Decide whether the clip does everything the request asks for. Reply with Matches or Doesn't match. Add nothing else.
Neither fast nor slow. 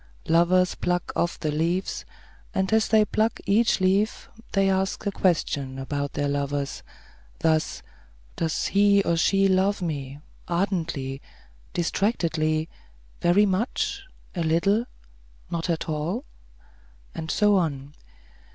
Doesn't match